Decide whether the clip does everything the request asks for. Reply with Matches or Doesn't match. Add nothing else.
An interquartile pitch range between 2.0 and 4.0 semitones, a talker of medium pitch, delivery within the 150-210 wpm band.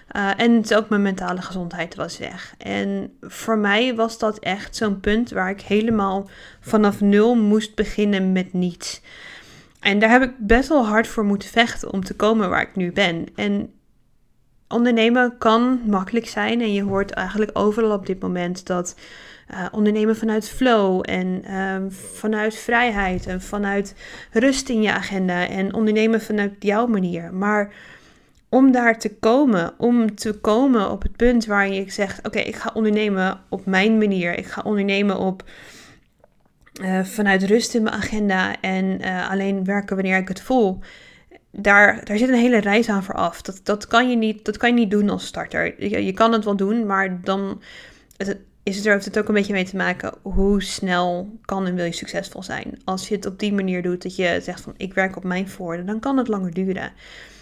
Doesn't match